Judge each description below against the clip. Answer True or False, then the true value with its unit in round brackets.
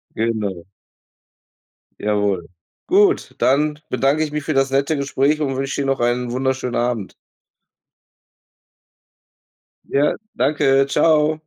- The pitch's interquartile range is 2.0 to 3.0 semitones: False (3.7 semitones)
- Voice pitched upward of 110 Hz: True (135 Hz)